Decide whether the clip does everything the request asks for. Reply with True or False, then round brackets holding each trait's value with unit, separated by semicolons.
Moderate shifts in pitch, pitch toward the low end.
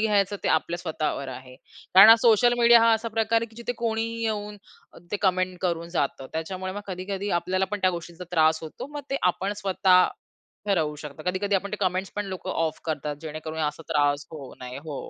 False (4.7 semitones; 185 Hz)